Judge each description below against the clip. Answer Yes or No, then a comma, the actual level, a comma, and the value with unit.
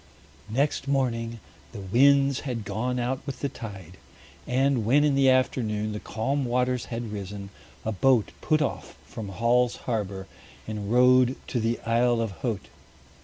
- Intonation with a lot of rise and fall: No, average, 3.3 semitones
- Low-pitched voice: Yes, low, 120 Hz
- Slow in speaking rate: No, average, 155 wpm